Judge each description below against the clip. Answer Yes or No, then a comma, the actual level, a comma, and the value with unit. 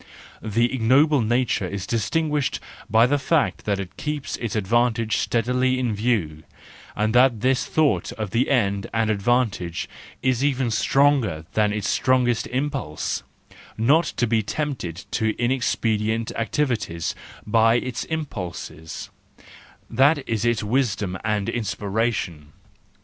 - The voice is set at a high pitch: No, low, 115 Hz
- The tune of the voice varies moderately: Yes, average, 3.7 semitones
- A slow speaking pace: Yes, slow, 120 wpm